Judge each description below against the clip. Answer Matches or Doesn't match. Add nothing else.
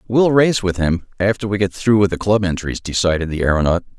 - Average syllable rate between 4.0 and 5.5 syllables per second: Doesn't match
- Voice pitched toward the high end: Doesn't match